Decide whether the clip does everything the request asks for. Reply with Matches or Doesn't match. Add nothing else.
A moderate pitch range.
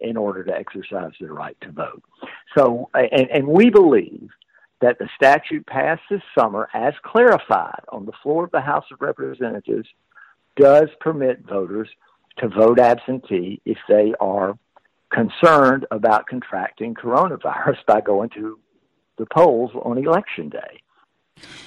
Doesn't match